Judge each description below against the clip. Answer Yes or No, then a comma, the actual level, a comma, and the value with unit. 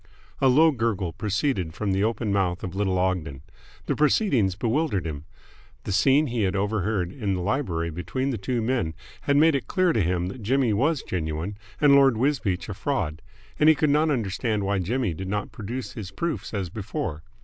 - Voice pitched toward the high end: No, low, 105 Hz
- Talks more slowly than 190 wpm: No, average, 195 wpm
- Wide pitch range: Yes, wide, 6.3 semitones